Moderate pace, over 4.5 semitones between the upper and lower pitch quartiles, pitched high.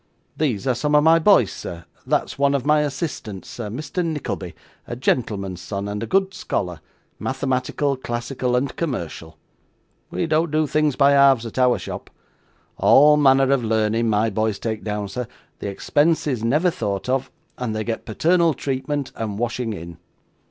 No: average, 170 wpm; average, 5.3 semitones; low, 125 Hz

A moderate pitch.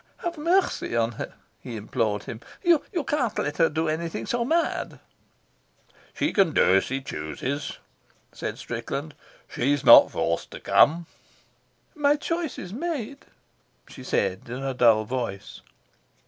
Yes: medium, 150 Hz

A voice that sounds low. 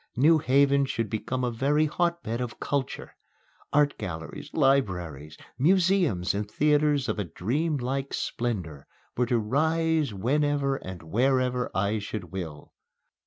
Yes: low, 130 Hz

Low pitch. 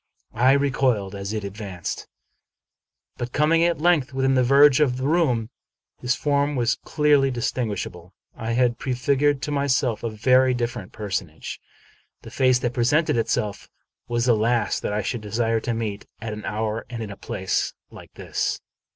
Yes: low, 120 Hz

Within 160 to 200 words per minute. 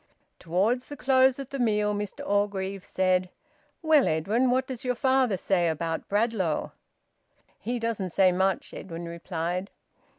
No: average, 140 wpm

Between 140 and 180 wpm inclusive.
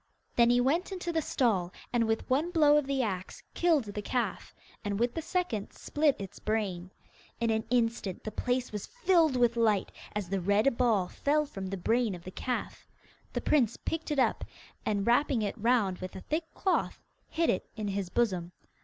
No: average, 195 wpm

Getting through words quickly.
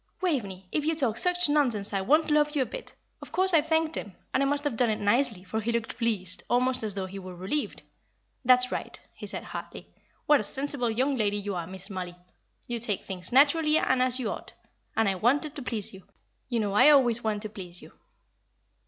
Yes: fast, 225 wpm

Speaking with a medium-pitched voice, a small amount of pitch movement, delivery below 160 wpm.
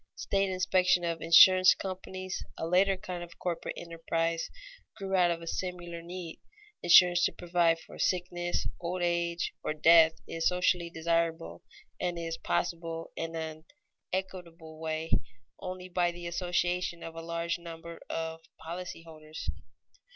Yes: medium, 170 Hz; narrow, 1.5 semitones; average, 140 wpm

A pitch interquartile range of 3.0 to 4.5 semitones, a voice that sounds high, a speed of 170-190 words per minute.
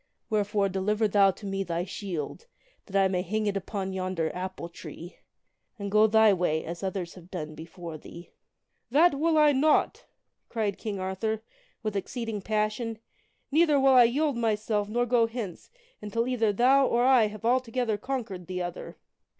Yes: average, 4.0 semitones; high, 210 Hz; average, 175 wpm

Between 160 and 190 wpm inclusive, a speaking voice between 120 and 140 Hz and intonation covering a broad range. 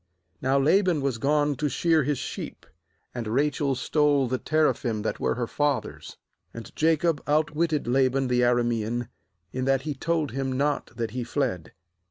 No: average, 165 wpm; low, 135 Hz; average, 3.5 semitones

